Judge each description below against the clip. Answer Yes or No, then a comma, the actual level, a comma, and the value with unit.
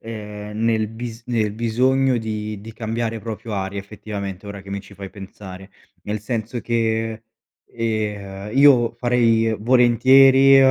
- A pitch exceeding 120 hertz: No, low, 110 Hz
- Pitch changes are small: Yes, narrow, 2.2 semitones